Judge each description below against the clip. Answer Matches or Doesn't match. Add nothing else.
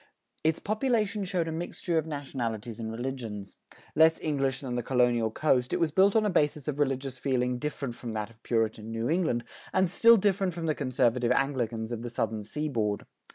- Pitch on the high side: Doesn't match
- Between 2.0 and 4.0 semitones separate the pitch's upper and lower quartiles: Doesn't match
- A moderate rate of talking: Matches